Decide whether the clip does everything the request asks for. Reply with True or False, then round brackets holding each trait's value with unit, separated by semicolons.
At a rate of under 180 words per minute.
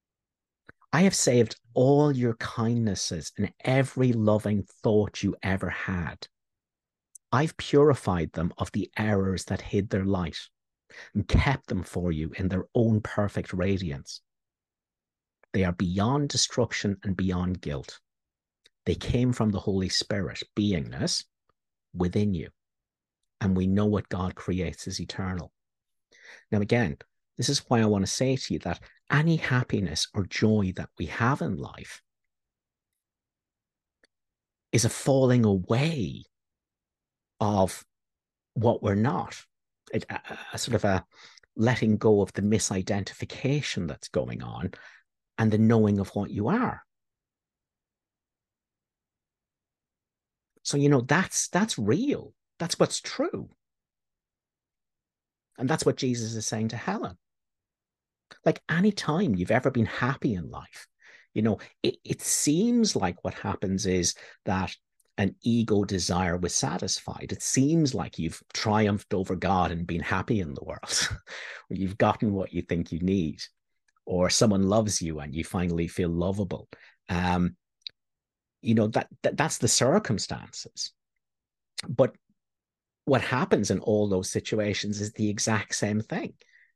True (135 wpm)